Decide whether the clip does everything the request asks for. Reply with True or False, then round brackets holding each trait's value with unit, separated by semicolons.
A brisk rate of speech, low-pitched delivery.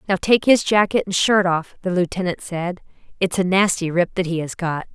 False (220 wpm; 185 Hz)